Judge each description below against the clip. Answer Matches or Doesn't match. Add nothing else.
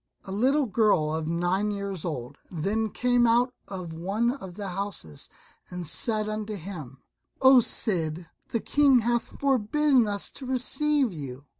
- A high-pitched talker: Matches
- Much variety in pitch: Matches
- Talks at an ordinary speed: Matches